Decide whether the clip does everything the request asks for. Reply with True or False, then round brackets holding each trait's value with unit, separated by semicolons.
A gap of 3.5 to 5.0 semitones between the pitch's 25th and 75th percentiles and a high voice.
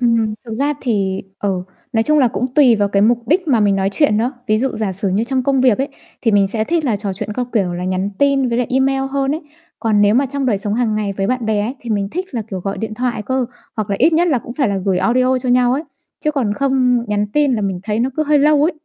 True (4.5 semitones; 235 Hz)